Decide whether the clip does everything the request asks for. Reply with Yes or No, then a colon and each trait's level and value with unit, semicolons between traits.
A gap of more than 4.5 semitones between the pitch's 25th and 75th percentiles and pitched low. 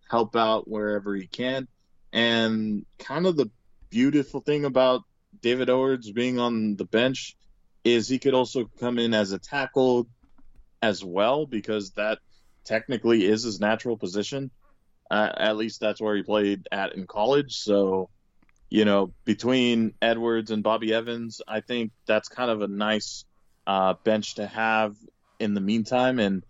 No: average, 2.7 semitones; low, 110 Hz